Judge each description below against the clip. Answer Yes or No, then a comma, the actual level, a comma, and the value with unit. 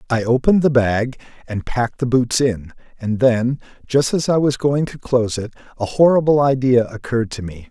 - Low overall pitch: Yes, low, 125 Hz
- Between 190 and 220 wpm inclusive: Yes, average, 195 wpm